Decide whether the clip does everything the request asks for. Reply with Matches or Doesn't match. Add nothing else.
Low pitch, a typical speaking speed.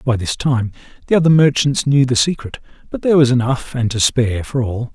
Doesn't match